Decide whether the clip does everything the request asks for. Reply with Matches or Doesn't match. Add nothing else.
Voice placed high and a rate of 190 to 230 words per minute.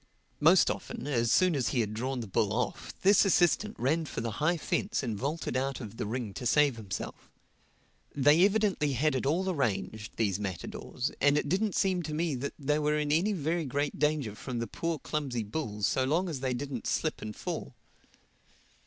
Doesn't match